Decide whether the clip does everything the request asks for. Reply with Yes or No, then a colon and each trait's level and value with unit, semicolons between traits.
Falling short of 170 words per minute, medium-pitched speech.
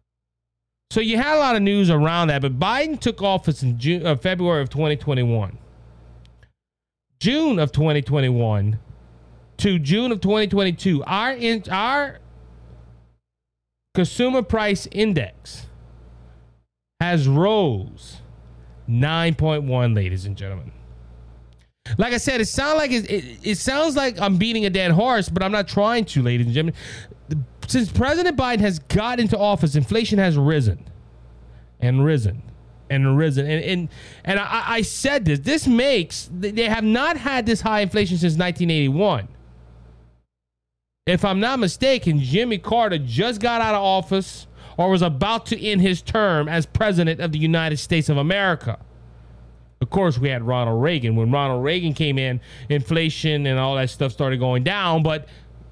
Yes: average, 150 wpm; medium, 155 Hz